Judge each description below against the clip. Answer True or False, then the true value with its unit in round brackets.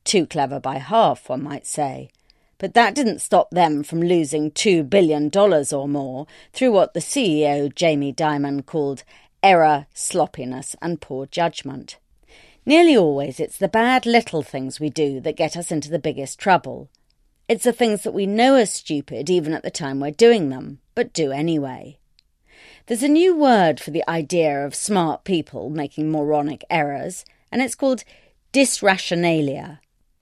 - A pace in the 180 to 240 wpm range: False (165 wpm)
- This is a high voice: False (160 Hz)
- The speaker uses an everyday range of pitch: False (5.7 semitones)